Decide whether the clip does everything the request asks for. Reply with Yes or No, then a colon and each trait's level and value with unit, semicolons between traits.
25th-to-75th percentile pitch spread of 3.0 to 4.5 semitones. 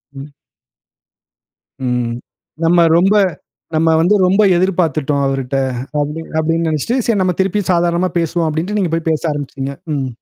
Yes: average, 3.9 semitones